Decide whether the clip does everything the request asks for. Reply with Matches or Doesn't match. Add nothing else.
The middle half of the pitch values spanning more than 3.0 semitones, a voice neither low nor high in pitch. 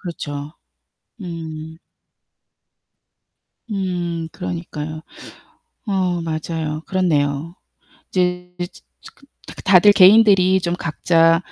Doesn't match